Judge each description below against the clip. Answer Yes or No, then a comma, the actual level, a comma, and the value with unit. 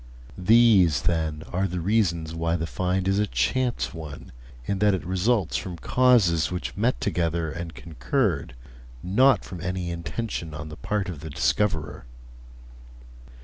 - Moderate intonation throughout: Yes, average, 4.0 semitones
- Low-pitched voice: Yes, very low, 90 Hz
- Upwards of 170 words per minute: No, average, 145 wpm